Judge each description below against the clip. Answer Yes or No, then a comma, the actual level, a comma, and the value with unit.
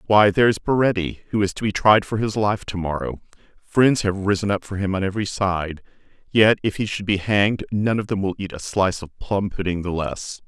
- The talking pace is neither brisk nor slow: No, fast, 230 wpm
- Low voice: Yes, low, 100 Hz